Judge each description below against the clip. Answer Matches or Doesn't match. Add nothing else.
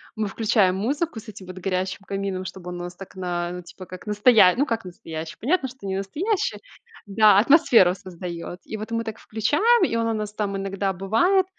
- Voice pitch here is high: Matches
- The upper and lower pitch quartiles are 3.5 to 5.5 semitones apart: Matches